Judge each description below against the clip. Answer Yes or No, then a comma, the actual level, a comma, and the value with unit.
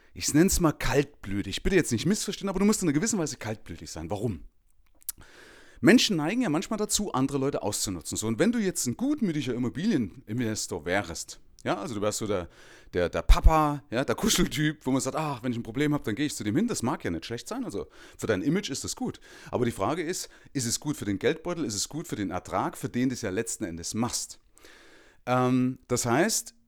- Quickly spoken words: Yes, fast, 235 wpm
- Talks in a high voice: No, low, 130 Hz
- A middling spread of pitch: No, wide, 6.3 semitones